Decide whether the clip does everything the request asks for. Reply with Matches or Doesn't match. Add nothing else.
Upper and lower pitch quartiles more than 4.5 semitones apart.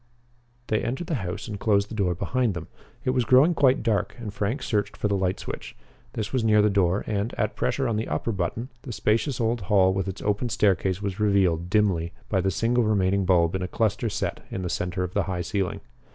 Doesn't match